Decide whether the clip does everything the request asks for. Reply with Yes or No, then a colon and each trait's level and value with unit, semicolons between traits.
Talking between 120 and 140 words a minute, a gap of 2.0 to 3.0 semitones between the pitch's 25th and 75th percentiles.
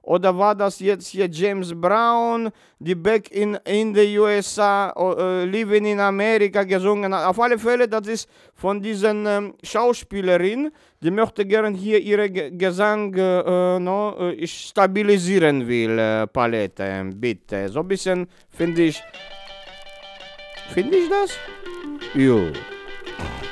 Yes: average, 130 wpm; average, 2.7 semitones